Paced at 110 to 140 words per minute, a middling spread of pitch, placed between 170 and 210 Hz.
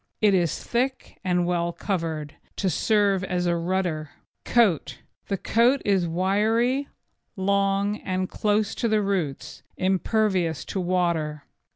Yes: slow, 135 wpm; average, 3.4 semitones; high, 190 Hz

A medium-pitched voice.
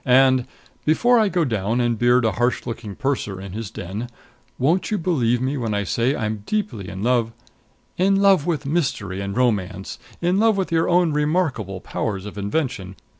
No: low, 125 Hz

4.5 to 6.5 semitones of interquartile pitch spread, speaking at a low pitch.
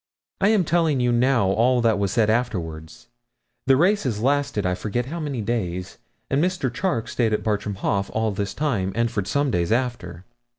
Yes: average, 5.2 semitones; low, 115 Hz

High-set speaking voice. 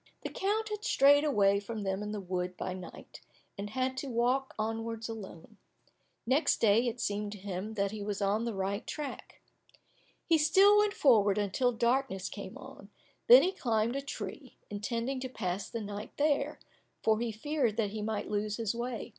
Yes: high, 225 Hz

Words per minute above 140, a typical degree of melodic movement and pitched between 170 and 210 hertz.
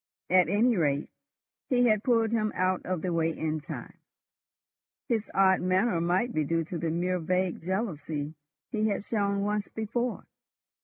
Yes: average, 160 wpm; average, 4.5 semitones; medium, 185 Hz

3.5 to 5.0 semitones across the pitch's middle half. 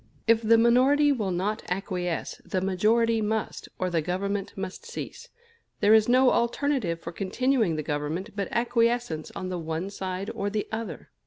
Yes: average, 4.2 semitones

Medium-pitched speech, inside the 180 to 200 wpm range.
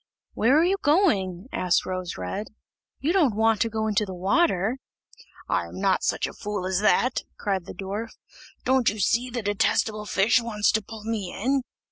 No: high, 215 Hz; average, 185 wpm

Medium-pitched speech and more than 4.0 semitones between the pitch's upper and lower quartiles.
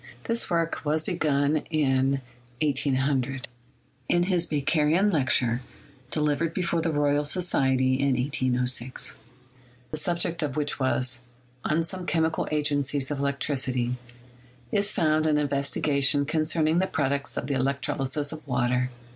No: medium, 145 Hz; average, 3.0 semitones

